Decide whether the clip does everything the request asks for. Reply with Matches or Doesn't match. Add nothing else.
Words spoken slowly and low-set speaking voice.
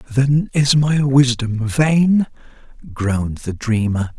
Matches